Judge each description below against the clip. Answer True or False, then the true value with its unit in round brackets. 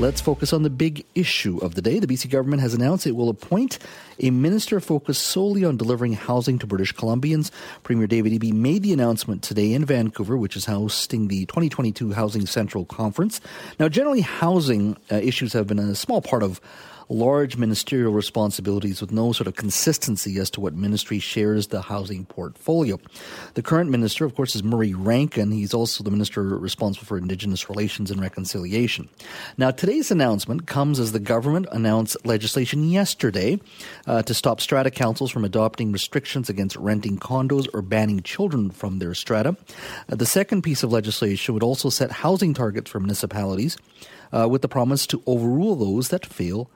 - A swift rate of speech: False (175 wpm)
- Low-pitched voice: True (115 Hz)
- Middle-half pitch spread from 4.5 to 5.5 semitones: True (5.1 semitones)